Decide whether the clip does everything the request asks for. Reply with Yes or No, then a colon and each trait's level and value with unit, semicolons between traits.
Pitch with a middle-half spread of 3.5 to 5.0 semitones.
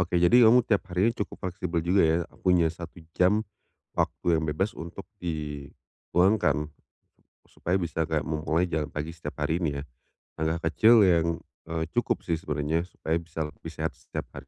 No: narrow, 2.4 semitones